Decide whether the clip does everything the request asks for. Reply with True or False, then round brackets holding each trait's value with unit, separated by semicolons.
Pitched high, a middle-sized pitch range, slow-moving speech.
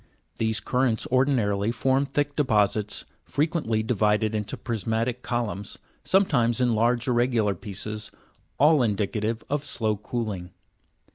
False (115 Hz; 3.2 semitones; 115 wpm)